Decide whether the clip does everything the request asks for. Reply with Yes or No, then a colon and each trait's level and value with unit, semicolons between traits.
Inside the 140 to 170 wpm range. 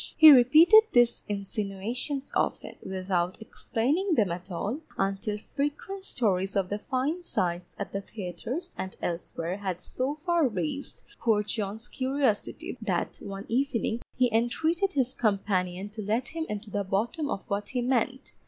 Yes: average, 150 wpm